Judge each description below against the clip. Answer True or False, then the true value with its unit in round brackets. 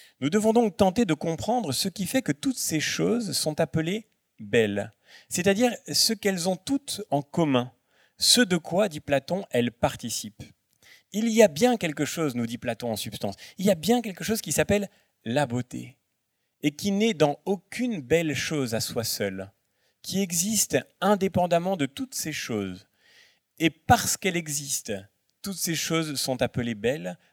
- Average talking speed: True (170 wpm)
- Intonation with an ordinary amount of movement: False (8.4 semitones)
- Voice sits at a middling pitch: True (165 Hz)